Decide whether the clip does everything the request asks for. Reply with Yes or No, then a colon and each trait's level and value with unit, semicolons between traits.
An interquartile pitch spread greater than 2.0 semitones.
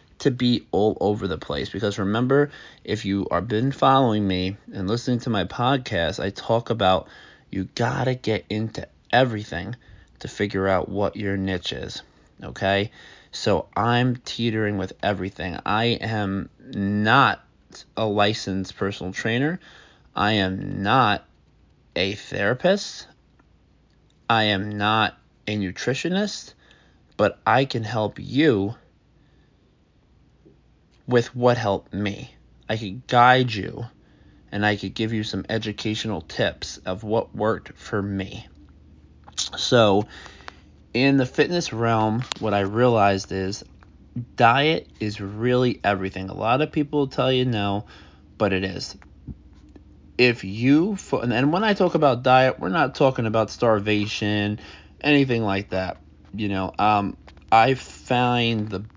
Yes: average, 4.1 semitones